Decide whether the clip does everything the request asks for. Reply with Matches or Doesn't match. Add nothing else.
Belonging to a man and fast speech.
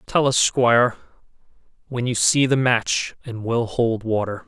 Doesn't match